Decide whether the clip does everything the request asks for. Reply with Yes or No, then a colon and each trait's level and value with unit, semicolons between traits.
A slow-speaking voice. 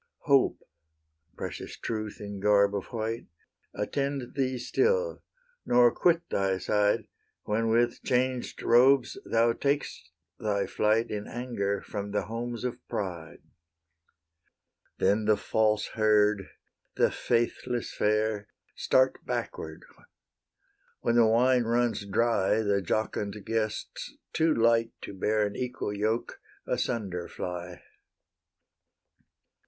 Yes: slow, 110 wpm